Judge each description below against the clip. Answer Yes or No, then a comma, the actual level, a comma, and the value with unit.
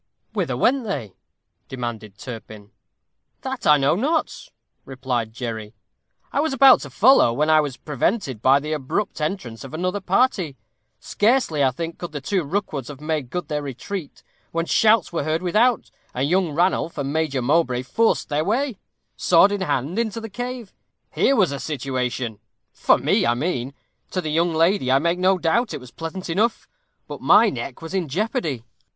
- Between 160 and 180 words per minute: Yes, average, 175 wpm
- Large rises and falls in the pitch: Yes, wide, 6.9 semitones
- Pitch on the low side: No, medium, 160 Hz